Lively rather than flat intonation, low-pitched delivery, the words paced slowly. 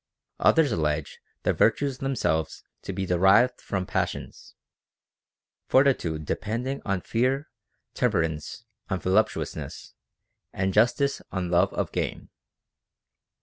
Yes: wide, 6.2 semitones; low, 100 Hz; slow, 105 wpm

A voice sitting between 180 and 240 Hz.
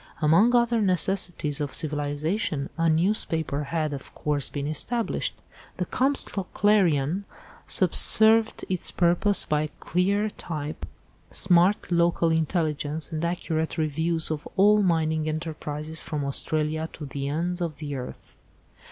No: medium, 160 Hz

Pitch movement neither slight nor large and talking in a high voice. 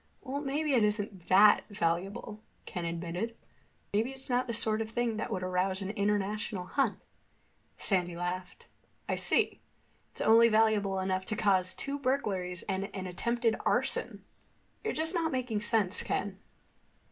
Yes: average, 3.9 semitones; high, 210 Hz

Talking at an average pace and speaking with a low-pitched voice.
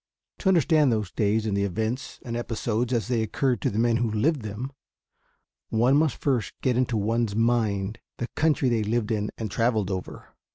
Yes: average, 190 wpm; low, 115 Hz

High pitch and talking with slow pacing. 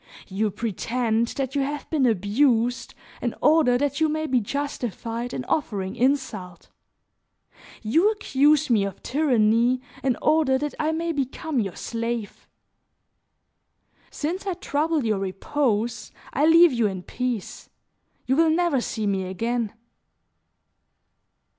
Yes: very high, 250 Hz; slow, 130 wpm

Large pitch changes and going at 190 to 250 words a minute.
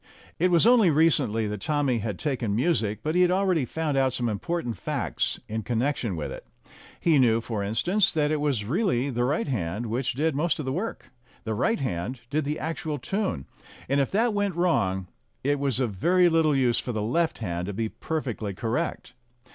Yes: wide, 6.3 semitones; average, 200 wpm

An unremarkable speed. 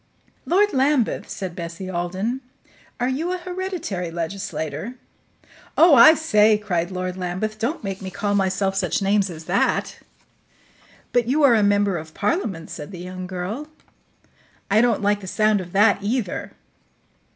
Yes: average, 150 wpm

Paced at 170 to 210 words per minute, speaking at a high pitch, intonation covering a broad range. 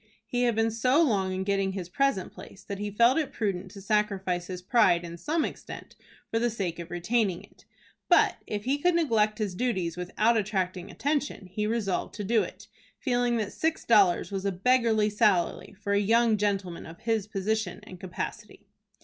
No: average, 190 wpm; high, 210 Hz; average, 3.8 semitones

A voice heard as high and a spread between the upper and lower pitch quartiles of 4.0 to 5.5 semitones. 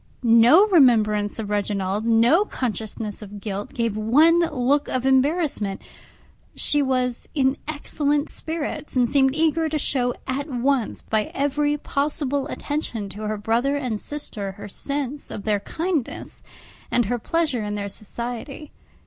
Yes: very high, 255 Hz; average, 5.2 semitones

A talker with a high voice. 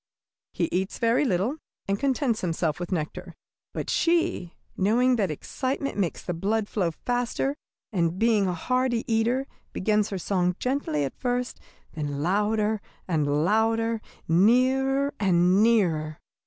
Yes: high, 210 Hz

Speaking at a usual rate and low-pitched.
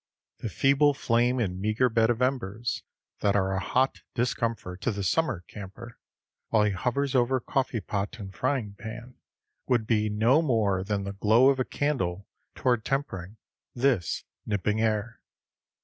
Yes: average, 155 wpm; low, 115 Hz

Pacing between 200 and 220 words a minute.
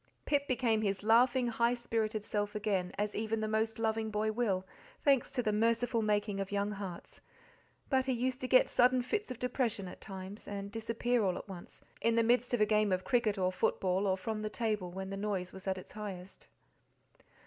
Yes: fast, 205 wpm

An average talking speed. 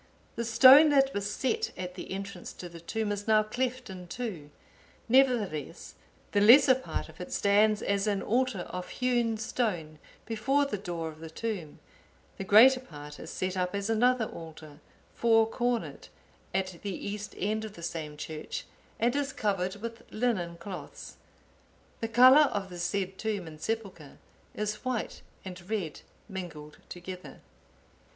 Yes: average, 160 wpm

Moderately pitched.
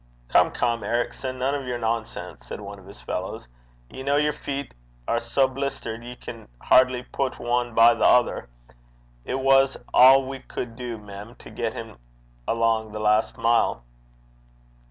No: low, 120 Hz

